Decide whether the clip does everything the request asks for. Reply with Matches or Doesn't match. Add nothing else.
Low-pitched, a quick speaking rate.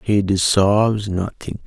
Doesn't match